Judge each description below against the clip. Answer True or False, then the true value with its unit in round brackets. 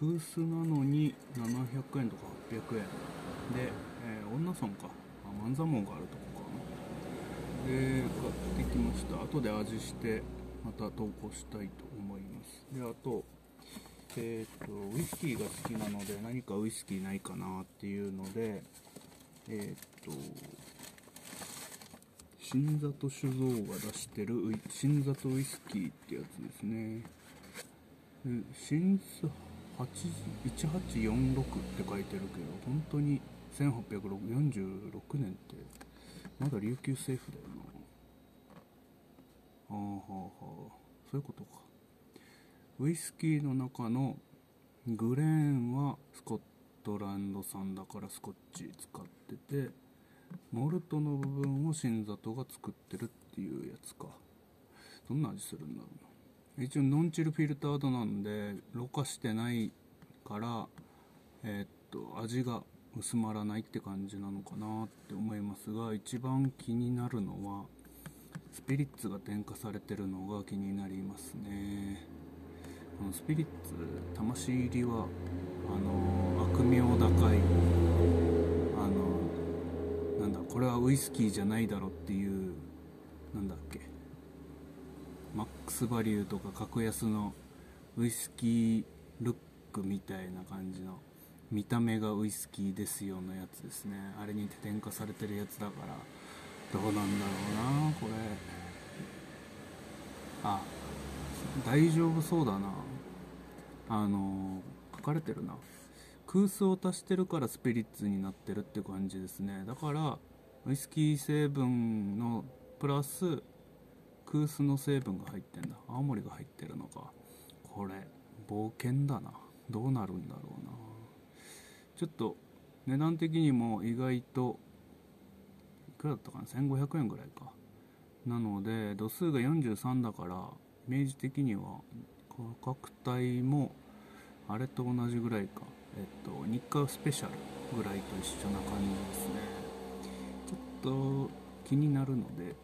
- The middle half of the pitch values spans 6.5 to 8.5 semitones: False (5.4 semitones)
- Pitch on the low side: True (110 Hz)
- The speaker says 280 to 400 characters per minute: False (235 characters per minute)